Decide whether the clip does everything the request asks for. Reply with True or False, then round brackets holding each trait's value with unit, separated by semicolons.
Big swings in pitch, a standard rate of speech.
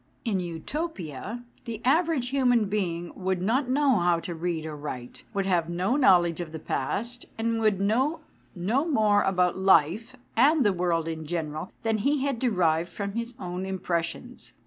True (6.0 semitones; 170 wpm)